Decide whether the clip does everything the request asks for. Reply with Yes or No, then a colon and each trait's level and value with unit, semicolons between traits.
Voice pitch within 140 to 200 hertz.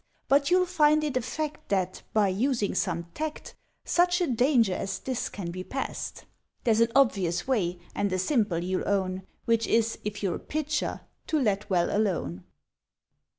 No: high, 220 Hz